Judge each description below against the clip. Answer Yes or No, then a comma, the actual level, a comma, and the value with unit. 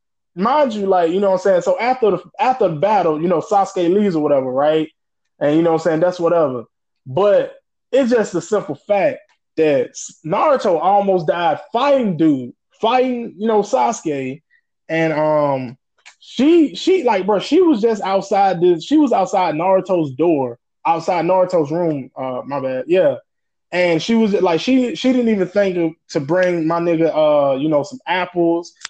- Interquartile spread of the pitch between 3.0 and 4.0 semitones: No, wide, 5.5 semitones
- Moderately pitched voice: Yes, medium, 180 Hz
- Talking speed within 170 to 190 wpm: Yes, average, 180 wpm